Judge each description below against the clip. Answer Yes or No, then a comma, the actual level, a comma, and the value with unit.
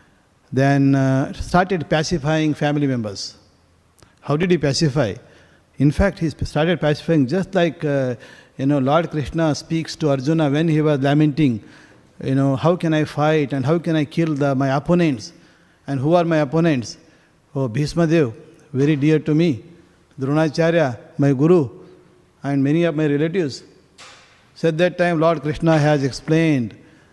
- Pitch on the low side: No, medium, 150 Hz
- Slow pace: No, average, 155 wpm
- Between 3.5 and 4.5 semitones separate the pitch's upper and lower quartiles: No, average, 2.9 semitones